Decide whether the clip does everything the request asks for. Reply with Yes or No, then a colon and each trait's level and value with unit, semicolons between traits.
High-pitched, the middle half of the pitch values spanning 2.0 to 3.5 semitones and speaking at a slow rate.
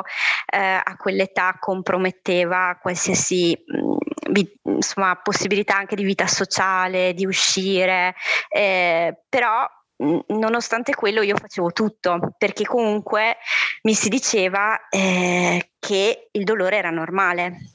Yes: high, 195 Hz; average, 2.8 semitones; slow, 105 wpm